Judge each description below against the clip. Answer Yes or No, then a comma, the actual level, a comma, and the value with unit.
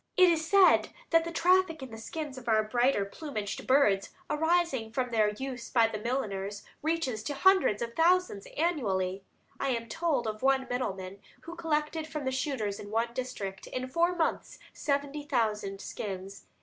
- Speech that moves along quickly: No, average, 170 wpm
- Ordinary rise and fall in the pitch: No, wide, 6.8 semitones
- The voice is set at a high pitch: Yes, very high, 255 Hz